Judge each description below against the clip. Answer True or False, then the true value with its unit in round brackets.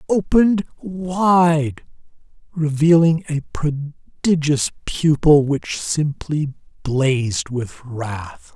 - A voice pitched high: False (150 Hz)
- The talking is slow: True (75 wpm)